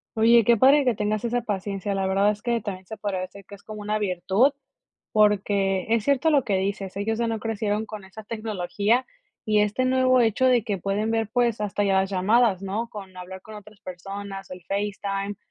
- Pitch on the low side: No, high, 210 Hz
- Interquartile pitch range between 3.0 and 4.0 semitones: No, narrow, 2.5 semitones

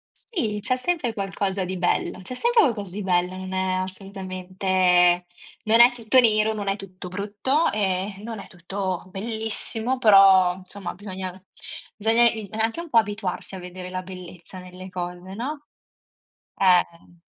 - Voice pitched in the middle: No, high, 195 Hz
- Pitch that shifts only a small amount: No, average, 3.1 semitones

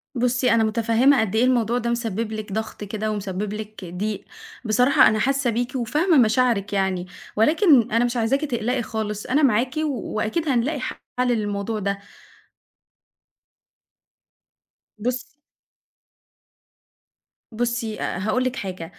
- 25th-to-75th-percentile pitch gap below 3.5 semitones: Yes, average, 3.0 semitones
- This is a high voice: Yes, high, 230 Hz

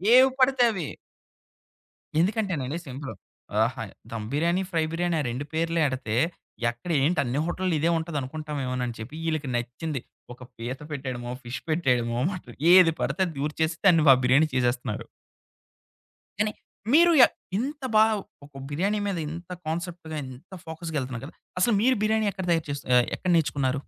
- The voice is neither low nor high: Yes, medium, 155 Hz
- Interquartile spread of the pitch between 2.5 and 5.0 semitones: No, wide, 5.5 semitones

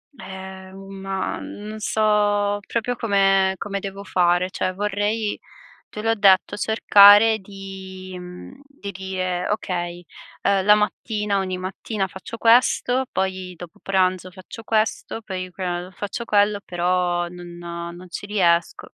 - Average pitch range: No, narrow, 2.2 semitones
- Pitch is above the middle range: Yes, high, 195 Hz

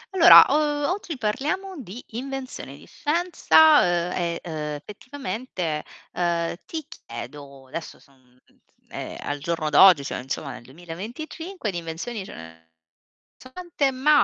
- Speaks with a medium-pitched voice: No, high, 195 Hz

